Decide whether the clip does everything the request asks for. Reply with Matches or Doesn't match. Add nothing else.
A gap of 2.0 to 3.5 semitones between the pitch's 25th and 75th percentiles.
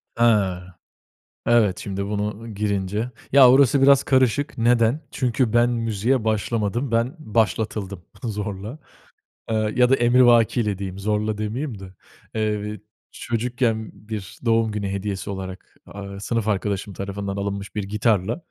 Matches